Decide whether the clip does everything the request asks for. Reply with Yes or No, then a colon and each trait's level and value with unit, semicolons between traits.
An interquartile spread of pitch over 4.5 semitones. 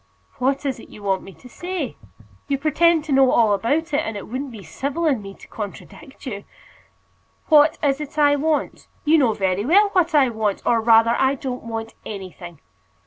Yes: average, 5.3 semitones